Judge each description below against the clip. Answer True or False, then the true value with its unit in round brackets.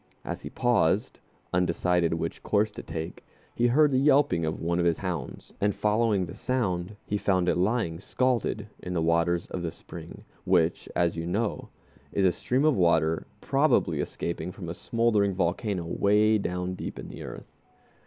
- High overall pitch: False (90 Hz)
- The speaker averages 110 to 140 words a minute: False (175 wpm)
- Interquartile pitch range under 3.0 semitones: False (4.0 semitones)